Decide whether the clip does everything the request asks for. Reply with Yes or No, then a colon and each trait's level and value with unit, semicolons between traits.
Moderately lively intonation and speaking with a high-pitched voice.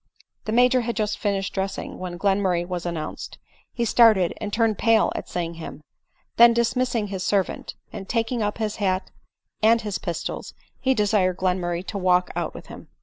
Yes: average, 3.7 semitones; high, 205 Hz